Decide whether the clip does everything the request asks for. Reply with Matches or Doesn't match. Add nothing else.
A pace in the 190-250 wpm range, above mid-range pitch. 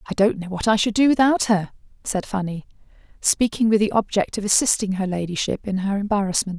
Matches